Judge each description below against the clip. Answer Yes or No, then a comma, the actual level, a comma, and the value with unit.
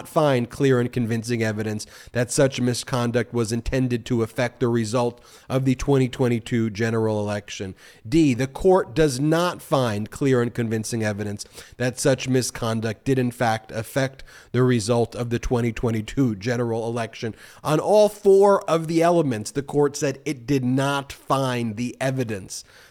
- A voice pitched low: Yes, low, 125 Hz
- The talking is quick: No, average, 150 wpm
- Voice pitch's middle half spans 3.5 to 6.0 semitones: No, average, 3.1 semitones